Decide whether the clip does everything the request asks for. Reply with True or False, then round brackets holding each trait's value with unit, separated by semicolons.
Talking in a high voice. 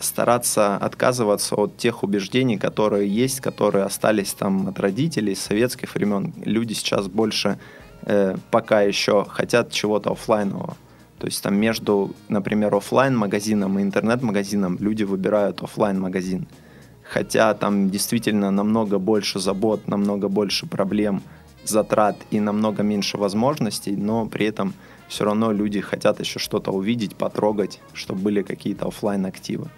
False (105 Hz)